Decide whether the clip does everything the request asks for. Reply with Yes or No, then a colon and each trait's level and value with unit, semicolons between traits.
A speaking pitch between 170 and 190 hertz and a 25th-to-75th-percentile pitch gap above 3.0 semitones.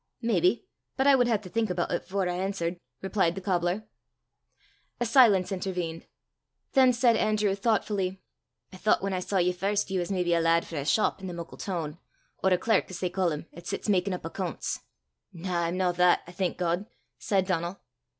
No: medium, 185 Hz; narrow, 2.5 semitones